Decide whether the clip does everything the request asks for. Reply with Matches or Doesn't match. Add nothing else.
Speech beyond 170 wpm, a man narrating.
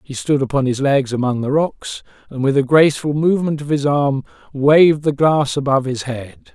Matches